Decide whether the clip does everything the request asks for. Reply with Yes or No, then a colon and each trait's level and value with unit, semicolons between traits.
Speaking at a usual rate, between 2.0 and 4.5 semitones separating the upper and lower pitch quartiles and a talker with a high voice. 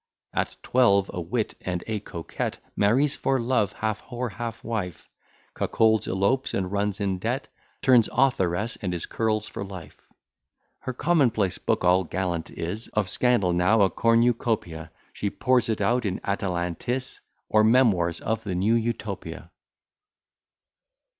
No: average, 145 wpm; average, 4.1 semitones; low, 105 Hz